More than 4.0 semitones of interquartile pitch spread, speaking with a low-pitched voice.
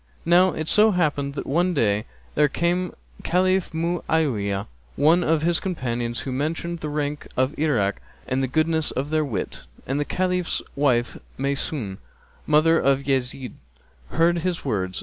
No: average, 4.6 semitones; medium, 150 Hz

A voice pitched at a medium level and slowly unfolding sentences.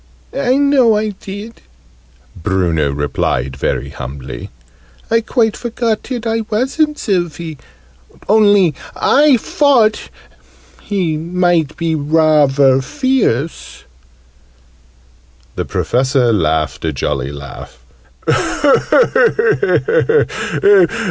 Yes: medium, 170 Hz; slow, 80 wpm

